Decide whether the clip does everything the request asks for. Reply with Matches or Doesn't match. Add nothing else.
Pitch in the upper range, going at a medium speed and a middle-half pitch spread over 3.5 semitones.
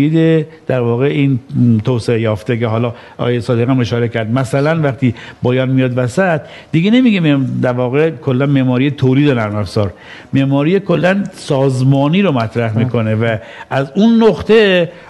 Doesn't match